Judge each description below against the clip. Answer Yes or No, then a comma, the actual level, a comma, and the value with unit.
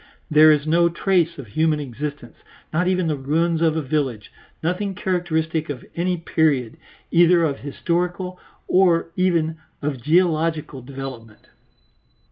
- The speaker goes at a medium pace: No, slow, 130 wpm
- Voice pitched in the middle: Yes, medium, 160 Hz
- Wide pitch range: No, average, 3.2 semitones